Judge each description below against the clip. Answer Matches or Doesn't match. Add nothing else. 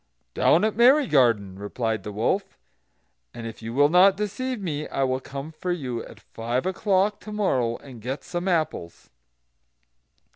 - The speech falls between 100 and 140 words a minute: Doesn't match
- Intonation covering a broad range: Matches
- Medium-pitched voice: Matches